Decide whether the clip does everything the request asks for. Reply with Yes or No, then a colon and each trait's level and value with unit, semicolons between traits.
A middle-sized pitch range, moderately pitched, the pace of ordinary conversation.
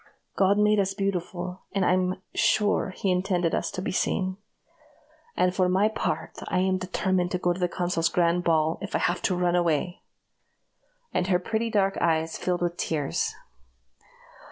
No: narrow, 1.6 semitones; medium, 180 Hz; average, 170 wpm